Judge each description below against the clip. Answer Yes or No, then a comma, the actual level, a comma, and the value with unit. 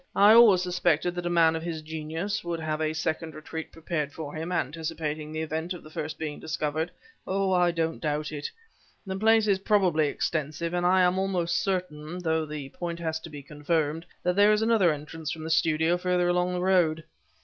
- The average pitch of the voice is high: No, medium, 165 Hz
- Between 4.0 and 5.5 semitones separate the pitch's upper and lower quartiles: No, narrow, 2.4 semitones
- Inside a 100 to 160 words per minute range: No, fast, 205 wpm